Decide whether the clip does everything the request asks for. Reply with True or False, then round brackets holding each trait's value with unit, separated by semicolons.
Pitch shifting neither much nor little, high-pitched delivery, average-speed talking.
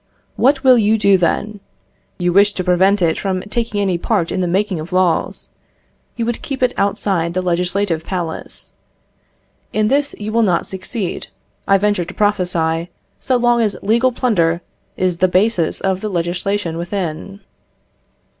True (3.4 semitones; 195 Hz; 160 wpm)